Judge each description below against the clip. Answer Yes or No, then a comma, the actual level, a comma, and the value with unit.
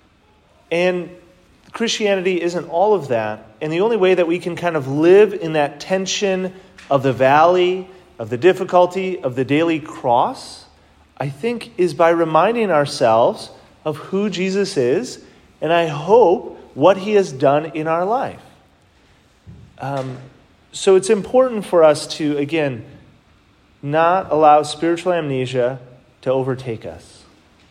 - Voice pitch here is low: No, medium, 160 Hz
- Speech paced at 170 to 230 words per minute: No, average, 140 wpm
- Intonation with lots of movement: Yes, wide, 5.7 semitones